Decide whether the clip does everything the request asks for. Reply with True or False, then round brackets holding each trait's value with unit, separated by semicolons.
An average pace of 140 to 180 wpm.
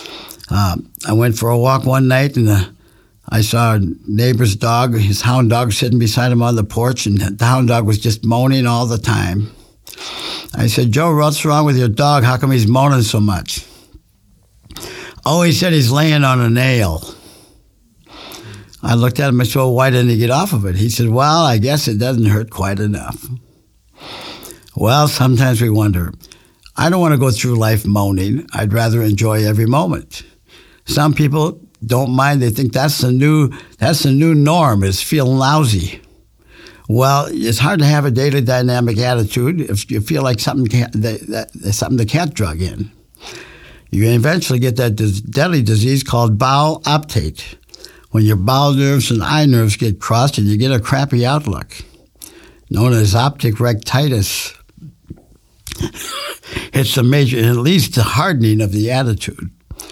True (175 wpm)